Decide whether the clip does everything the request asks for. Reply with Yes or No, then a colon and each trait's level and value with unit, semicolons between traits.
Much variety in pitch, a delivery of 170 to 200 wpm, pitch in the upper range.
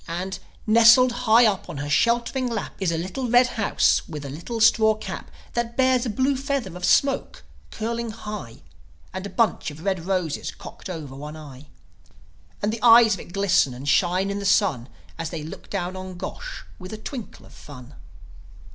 Yes: wide, 5.9 semitones; average, 190 wpm; high, 200 Hz